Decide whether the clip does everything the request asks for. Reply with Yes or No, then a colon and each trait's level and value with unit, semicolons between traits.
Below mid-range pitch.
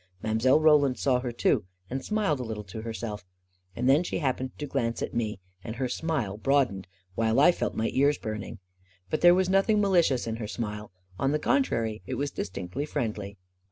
Yes: low, 125 Hz